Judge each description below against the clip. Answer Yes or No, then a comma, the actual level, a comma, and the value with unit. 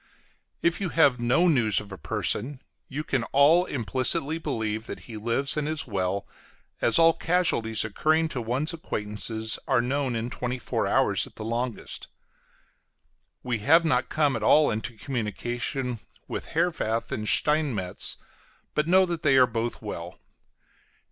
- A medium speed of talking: Yes, average, 155 wpm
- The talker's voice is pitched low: Yes, low, 125 Hz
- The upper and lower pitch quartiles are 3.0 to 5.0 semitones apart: No, wide, 5.4 semitones